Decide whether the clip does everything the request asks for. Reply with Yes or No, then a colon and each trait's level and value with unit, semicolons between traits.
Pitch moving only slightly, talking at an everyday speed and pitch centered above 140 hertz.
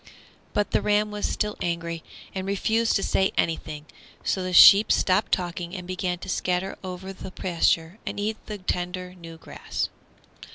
Yes: narrow, 2.2 semitones; average, 165 wpm; medium, 185 Hz